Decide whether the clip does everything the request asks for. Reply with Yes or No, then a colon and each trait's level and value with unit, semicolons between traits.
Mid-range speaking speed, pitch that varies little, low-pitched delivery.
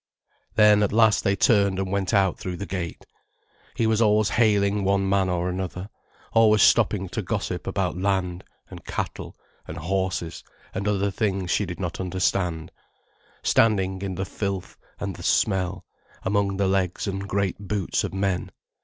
Yes: average, 160 wpm; narrow, 1.6 semitones; very low, 95 Hz